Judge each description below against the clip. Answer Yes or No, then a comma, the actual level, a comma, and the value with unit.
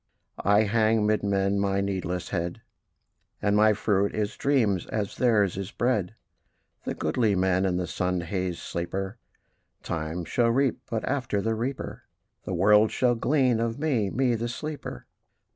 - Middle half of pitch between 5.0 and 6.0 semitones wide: No, average, 3.7 semitones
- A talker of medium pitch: No, low, 105 Hz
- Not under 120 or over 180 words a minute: Yes, average, 155 wpm